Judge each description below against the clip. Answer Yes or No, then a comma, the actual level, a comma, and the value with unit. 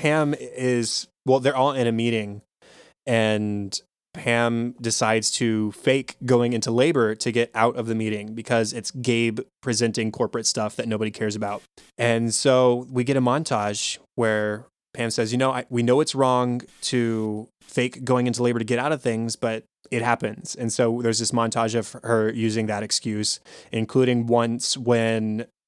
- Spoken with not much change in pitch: Yes, narrow, 2.0 semitones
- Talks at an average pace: Yes, average, 175 wpm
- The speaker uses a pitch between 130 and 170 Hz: No, low, 115 Hz